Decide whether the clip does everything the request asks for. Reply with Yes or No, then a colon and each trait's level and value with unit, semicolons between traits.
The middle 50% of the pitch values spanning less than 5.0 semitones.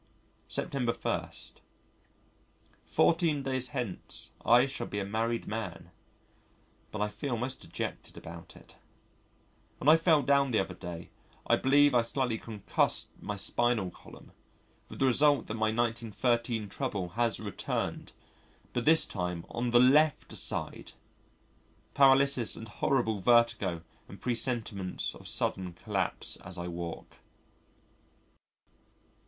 Yes: average, 4.3 semitones